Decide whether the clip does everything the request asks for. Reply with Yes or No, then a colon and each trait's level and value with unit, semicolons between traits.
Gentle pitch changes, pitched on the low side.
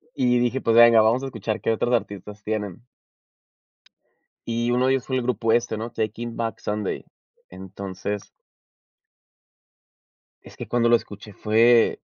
Yes: narrow, 2.3 semitones; low, 115 Hz